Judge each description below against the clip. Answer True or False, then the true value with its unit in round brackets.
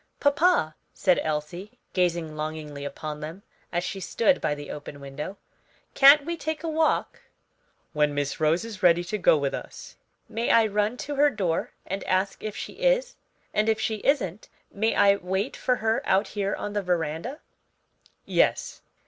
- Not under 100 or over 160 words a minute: False (170 wpm)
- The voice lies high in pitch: True (195 Hz)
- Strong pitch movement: True (6.6 semitones)